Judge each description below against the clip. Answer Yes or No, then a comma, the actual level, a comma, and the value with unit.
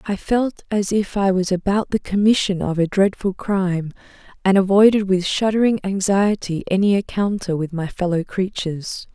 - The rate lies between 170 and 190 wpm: No, average, 160 wpm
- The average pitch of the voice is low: No, high, 195 Hz